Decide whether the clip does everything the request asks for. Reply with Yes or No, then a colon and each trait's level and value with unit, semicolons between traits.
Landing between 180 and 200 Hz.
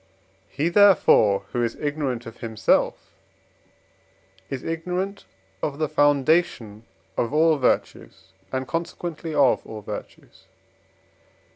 No: medium, 145 Hz